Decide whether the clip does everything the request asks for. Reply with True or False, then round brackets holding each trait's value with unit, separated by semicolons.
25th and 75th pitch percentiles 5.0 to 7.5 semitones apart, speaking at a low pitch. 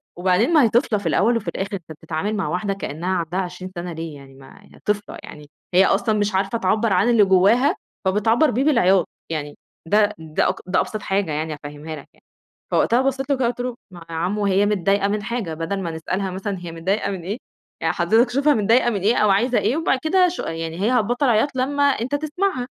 False (5.3 semitones; 200 Hz)